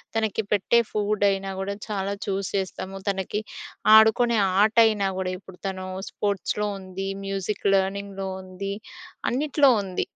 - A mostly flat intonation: Yes, narrow, 1.7 semitones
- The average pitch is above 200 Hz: No, high, 195 Hz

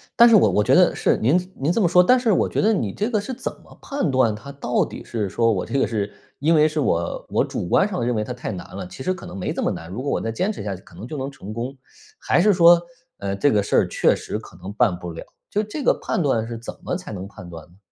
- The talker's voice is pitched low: Yes, low, 125 Hz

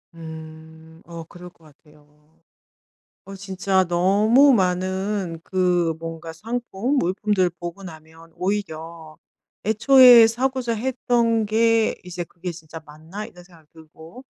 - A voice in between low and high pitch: Yes, medium, 180 Hz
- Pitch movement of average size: Yes, average, 4.9 semitones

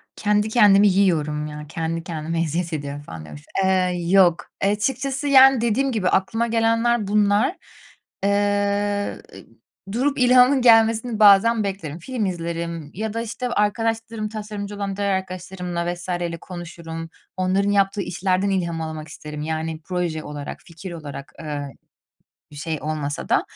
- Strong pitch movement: No, average, 4.6 semitones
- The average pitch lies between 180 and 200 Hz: Yes, high, 190 Hz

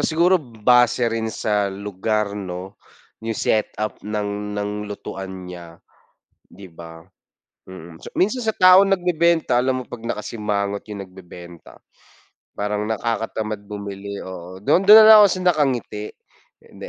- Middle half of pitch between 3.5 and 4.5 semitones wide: Yes, average, 4.1 semitones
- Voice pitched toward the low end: Yes, low, 105 Hz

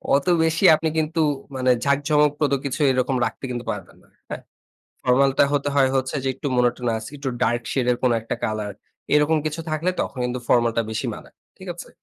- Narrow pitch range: No, average, 3.3 semitones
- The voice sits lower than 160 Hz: Yes, low, 135 Hz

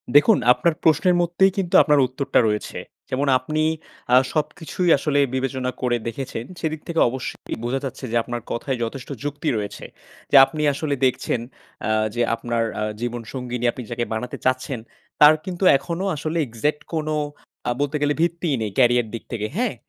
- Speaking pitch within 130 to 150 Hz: Yes, low, 135 Hz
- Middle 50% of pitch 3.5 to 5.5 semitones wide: Yes, average, 4.2 semitones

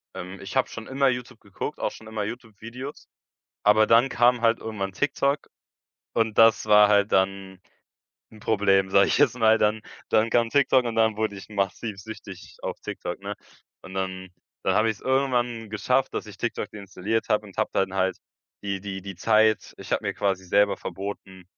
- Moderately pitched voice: No, low, 110 Hz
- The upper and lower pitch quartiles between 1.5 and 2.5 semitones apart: No, average, 2.9 semitones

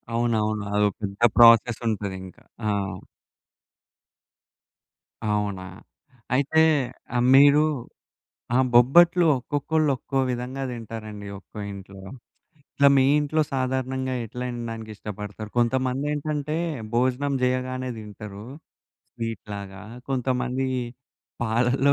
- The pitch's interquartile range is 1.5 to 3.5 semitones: No, average, 4.0 semitones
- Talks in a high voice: No, low, 120 Hz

